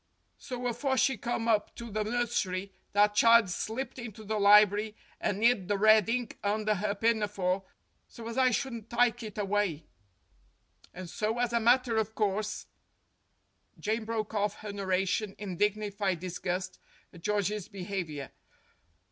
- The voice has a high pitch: Yes, high, 210 Hz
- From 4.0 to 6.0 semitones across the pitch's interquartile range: No, narrow, 2.5 semitones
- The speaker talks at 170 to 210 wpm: No, average, 150 wpm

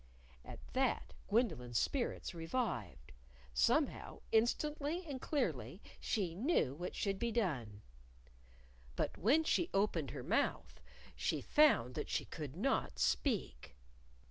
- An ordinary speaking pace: No, slow, 115 wpm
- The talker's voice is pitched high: Yes, high, 210 Hz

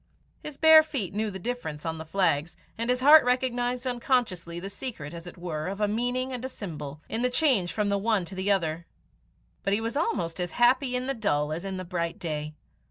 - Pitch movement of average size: No, wide, 6.6 semitones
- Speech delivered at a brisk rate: Yes, fast, 225 wpm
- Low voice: No, high, 205 Hz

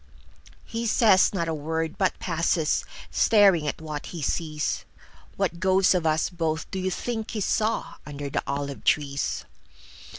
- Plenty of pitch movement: No, average, 3.9 semitones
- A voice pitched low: No, medium, 165 Hz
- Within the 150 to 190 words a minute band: No, slow, 135 wpm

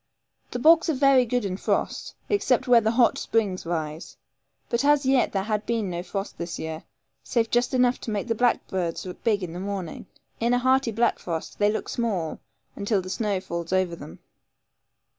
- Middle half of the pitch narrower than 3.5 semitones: No, average, 5.0 semitones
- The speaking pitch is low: No, high, 215 Hz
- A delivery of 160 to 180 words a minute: No, average, 195 wpm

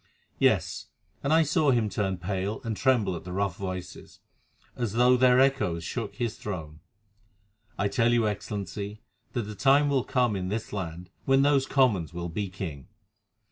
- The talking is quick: No, average, 170 wpm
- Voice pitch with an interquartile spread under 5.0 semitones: No, wide, 5.4 semitones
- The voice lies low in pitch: Yes, low, 105 Hz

